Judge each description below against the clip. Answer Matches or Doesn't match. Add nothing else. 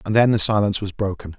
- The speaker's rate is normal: Doesn't match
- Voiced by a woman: Doesn't match